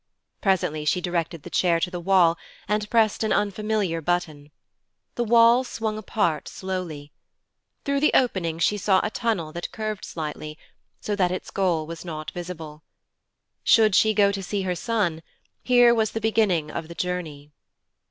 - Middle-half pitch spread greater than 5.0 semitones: No, average, 4.5 semitones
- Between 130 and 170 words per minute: Yes, average, 160 wpm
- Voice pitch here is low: No, medium, 185 Hz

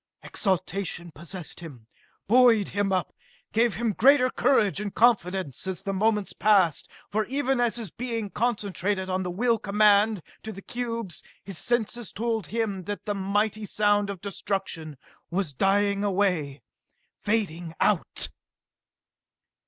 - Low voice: No, high, 205 Hz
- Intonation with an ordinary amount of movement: Yes, average, 3.0 semitones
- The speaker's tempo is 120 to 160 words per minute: Yes, slow, 135 wpm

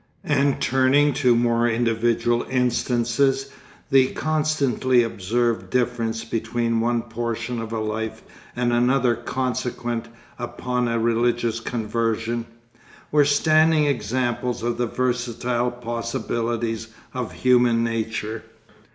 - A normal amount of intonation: No, narrow, 1.6 semitones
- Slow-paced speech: Yes, slow, 110 wpm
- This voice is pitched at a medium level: No, low, 120 Hz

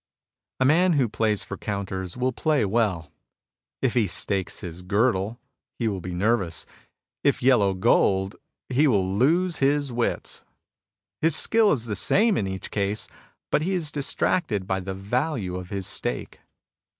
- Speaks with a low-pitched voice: Yes, low, 110 Hz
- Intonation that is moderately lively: No, wide, 6.4 semitones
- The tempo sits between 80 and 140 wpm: No, average, 155 wpm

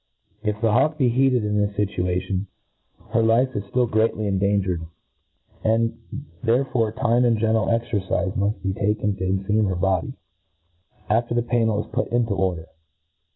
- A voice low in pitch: Yes, low, 110 Hz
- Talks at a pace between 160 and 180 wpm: Yes, average, 165 wpm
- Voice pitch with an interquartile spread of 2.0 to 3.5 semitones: Yes, average, 3.0 semitones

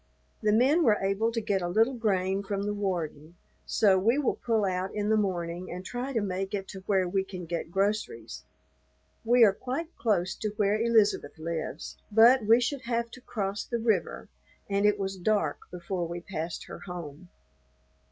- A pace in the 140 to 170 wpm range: No, average, 185 wpm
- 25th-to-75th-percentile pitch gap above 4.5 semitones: No, average, 3.8 semitones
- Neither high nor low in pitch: No, high, 200 Hz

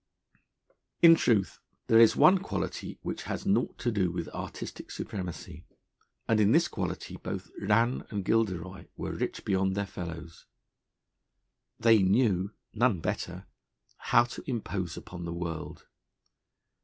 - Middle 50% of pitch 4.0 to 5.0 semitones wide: Yes, average, 4.6 semitones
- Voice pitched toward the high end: No, low, 100 Hz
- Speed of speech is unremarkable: No, slow, 130 wpm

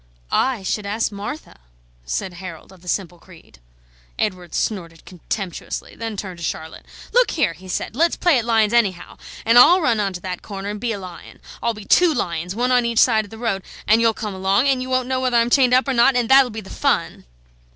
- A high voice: Yes, high, 215 Hz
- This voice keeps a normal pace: No, fast, 225 wpm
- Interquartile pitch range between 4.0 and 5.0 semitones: Yes, average, 4.7 semitones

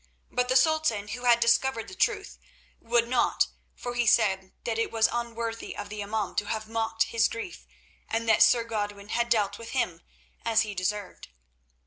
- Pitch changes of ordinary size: No, narrow, 2.3 semitones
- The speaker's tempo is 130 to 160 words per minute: No, average, 180 wpm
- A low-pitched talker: No, high, 225 Hz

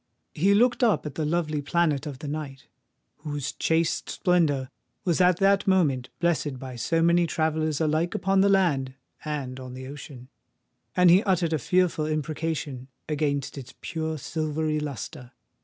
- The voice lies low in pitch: No, medium, 155 Hz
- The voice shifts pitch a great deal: No, average, 3.4 semitones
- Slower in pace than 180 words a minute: Yes, average, 155 wpm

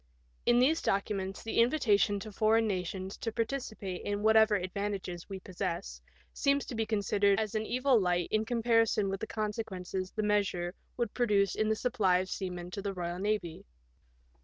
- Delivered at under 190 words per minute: Yes, average, 170 wpm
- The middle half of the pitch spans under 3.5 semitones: Yes, average, 2.8 semitones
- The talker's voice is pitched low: No, high, 205 Hz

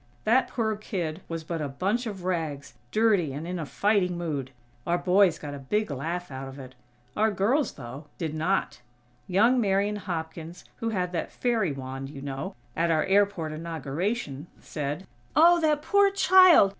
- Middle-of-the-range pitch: Yes, medium, 175 Hz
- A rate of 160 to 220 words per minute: Yes, average, 170 wpm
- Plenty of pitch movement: Yes, wide, 5.9 semitones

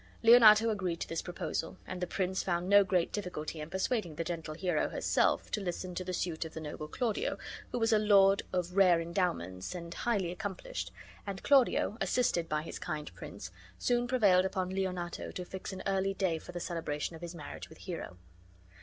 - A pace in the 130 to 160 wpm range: No, average, 195 wpm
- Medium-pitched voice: Yes, medium, 180 Hz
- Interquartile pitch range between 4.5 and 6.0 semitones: No, average, 2.9 semitones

